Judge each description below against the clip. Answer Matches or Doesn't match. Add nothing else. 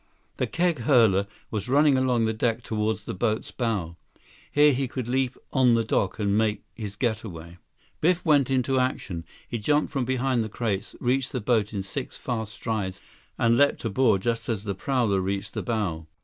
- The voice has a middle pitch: Doesn't match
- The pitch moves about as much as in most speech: Matches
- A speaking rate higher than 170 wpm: Matches